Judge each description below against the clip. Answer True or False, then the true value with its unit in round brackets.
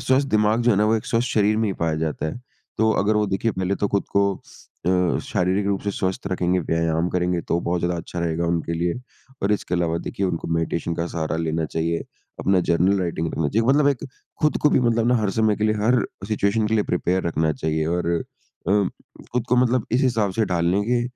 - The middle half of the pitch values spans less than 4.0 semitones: False (4.4 semitones)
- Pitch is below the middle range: True (95 Hz)